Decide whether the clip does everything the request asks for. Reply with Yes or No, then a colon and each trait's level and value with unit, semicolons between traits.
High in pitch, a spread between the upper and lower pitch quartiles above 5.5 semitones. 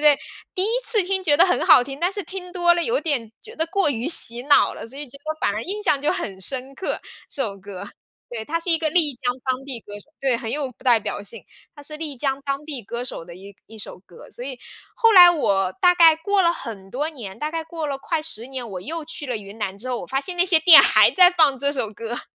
Yes: very high, 280 Hz; wide, 6.2 semitones